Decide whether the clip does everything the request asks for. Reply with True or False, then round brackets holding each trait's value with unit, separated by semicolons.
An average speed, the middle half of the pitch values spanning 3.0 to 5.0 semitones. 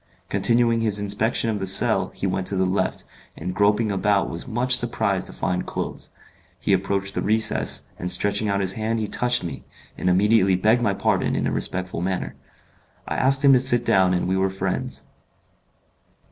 True (190 wpm; 3.3 semitones)